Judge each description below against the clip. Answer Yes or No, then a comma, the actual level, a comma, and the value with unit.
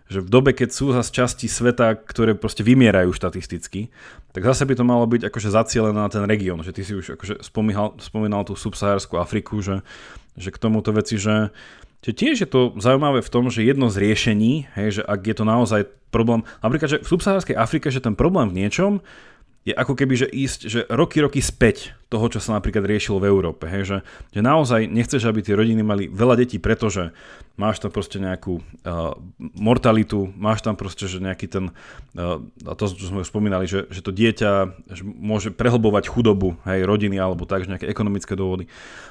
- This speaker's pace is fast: Yes, fast, 200 wpm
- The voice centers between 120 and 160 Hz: No, low, 105 Hz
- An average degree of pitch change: Yes, average, 3.5 semitones